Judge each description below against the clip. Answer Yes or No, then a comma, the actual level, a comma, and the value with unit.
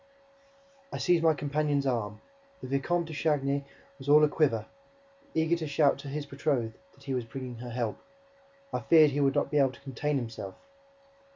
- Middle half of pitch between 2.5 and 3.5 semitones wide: Yes, average, 3.0 semitones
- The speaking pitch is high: No, medium, 140 Hz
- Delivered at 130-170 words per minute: No, average, 190 wpm